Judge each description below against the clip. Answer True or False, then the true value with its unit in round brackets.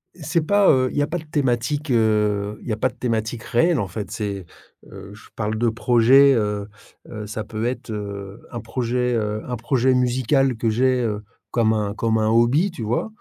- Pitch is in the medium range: False (115 Hz)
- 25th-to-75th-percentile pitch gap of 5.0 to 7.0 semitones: False (3.2 semitones)